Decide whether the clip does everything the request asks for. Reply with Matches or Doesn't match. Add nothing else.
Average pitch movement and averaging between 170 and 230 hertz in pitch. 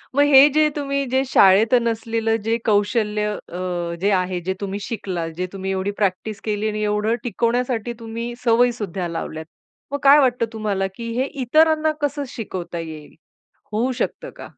Matches